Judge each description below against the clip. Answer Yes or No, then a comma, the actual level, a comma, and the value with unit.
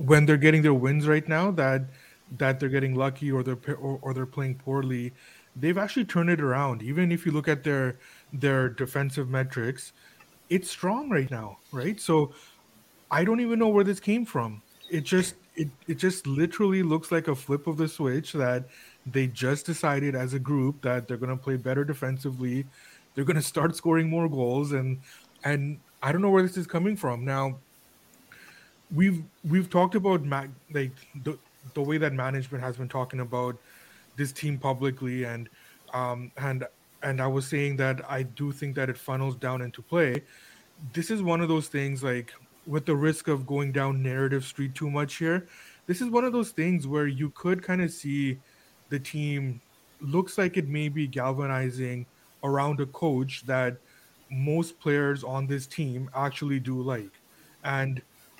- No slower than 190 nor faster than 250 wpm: No, average, 180 wpm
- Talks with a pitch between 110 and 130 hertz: No, medium, 140 Hz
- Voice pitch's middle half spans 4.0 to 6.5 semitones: No, average, 3.4 semitones